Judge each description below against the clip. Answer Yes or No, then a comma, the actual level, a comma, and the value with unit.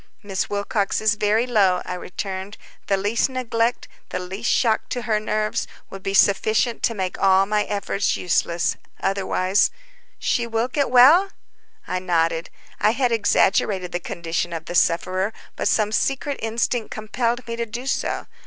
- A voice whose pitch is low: No, high, 210 Hz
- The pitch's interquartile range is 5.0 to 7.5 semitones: No, average, 3.7 semitones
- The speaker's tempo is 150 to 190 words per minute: Yes, average, 160 wpm